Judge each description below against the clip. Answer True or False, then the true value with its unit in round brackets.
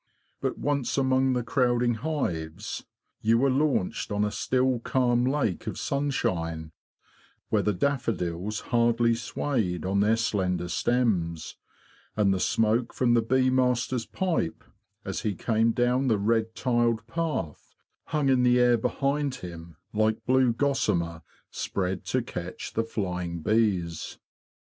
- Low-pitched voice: True (115 Hz)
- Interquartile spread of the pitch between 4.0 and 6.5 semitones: True (5.0 semitones)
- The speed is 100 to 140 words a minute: True (135 wpm)